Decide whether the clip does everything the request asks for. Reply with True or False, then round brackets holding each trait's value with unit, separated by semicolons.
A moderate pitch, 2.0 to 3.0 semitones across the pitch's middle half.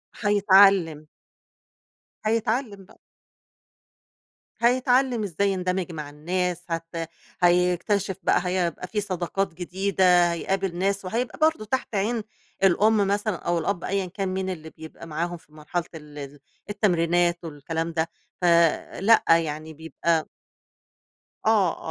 False (180 Hz; 3.4 semitones)